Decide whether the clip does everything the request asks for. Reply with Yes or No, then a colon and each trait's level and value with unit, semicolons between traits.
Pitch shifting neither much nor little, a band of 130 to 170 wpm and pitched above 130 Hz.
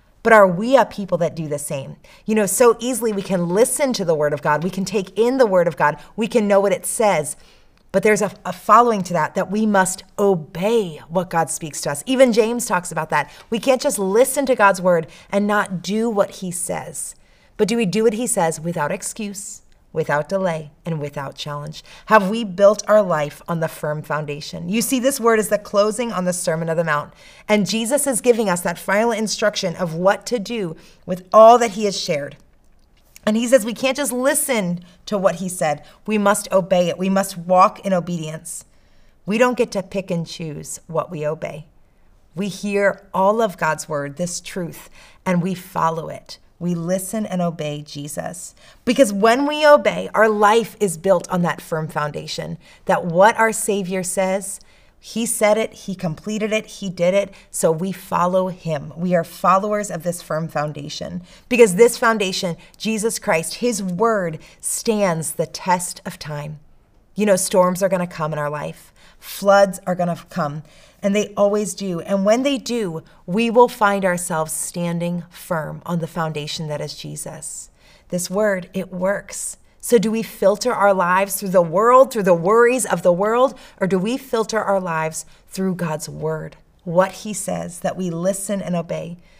No: average, 4.1 semitones; average, 195 wpm; high, 190 Hz